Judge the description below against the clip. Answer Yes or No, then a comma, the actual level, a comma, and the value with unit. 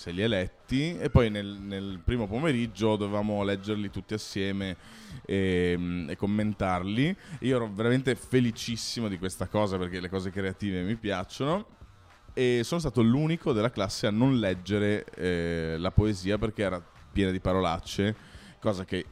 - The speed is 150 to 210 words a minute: Yes, average, 155 wpm